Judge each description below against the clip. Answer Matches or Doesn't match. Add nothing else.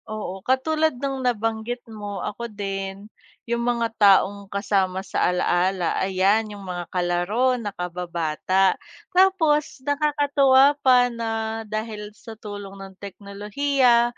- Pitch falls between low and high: Doesn't match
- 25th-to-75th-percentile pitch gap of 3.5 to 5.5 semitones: Matches